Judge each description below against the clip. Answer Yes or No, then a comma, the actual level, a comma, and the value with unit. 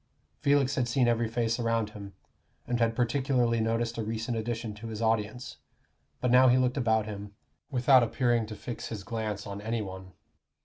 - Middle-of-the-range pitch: No, low, 115 Hz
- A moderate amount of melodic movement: No, narrow, 2.2 semitones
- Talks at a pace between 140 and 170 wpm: No, average, 180 wpm